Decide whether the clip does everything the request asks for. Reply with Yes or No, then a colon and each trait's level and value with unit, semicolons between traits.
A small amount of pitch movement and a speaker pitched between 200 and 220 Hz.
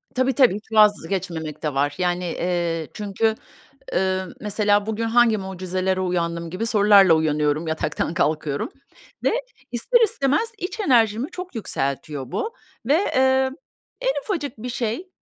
No: wide, 6.4 semitones; high, 205 Hz